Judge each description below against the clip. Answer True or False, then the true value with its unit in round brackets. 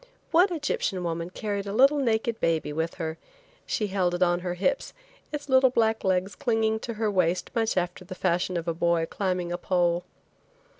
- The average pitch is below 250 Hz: True (185 Hz)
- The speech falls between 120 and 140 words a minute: False (190 wpm)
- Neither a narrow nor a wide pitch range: True (4.2 semitones)